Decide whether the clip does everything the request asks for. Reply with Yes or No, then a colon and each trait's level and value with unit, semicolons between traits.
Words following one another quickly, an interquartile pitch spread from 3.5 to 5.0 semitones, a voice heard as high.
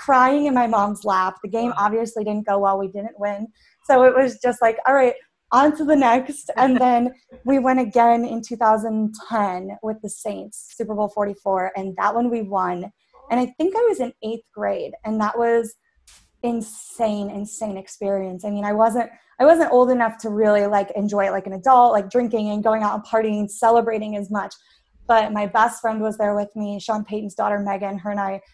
No: fast, 210 wpm; average, 2.8 semitones; high, 220 Hz